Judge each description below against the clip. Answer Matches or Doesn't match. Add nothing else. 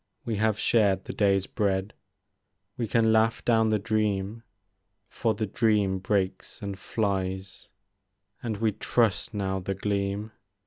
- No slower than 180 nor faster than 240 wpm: Doesn't match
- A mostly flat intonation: Matches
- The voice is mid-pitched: Doesn't match